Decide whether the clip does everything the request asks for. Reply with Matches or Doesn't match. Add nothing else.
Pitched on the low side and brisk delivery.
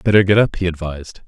Matches